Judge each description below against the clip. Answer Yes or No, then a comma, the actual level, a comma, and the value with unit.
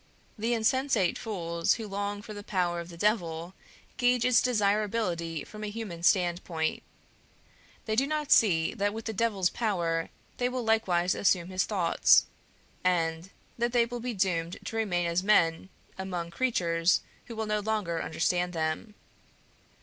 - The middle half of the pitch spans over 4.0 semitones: Yes, average, 4.6 semitones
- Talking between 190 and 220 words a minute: No, average, 155 wpm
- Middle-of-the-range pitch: No, high, 195 Hz